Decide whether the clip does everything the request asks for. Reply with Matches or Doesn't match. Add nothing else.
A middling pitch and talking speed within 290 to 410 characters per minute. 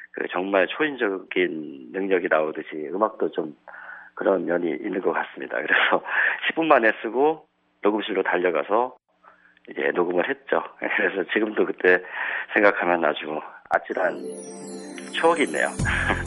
Doesn't match